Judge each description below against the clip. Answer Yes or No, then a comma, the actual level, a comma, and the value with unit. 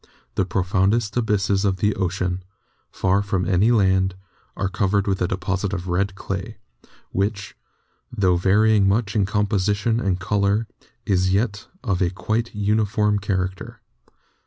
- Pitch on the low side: Yes, low, 100 Hz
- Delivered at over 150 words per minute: No, slow, 135 wpm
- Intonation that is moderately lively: No, narrow, 1.8 semitones